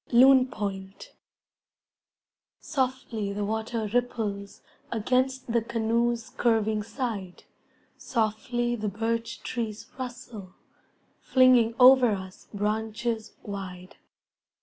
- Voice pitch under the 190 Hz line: No, high, 225 Hz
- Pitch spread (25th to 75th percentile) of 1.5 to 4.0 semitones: Yes, narrow, 2.6 semitones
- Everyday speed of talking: No, slow, 85 wpm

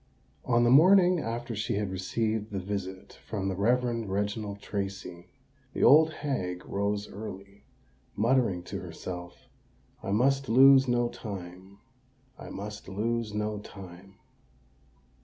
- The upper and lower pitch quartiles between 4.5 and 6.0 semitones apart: No, average, 3.9 semitones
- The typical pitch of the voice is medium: No, low, 105 Hz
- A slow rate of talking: Yes, slow, 120 wpm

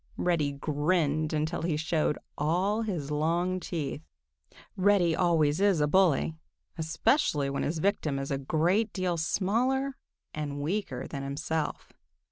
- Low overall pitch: No, medium, 160 Hz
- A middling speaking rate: No, slow, 130 wpm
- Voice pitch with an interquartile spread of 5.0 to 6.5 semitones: No, average, 3.9 semitones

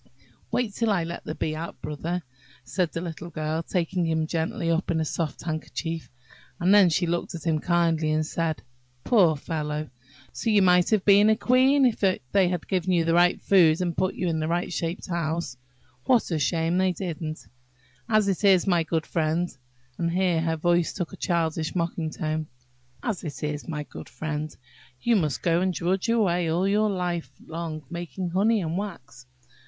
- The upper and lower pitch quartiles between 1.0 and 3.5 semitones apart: Yes, average, 2.8 semitones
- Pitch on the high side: No, medium, 170 Hz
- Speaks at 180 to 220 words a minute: Yes, average, 190 wpm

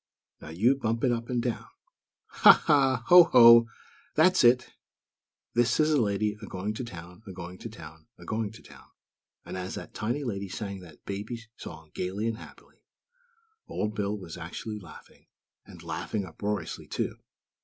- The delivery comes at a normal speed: Yes, average, 170 wpm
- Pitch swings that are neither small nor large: Yes, average, 4.1 semitones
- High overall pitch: No, low, 105 Hz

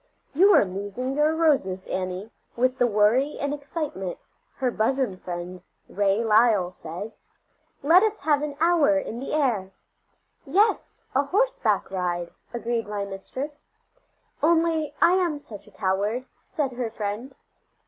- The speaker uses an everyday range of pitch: No, wide, 6.9 semitones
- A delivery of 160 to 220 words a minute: No, average, 140 wpm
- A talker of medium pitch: No, high, 245 Hz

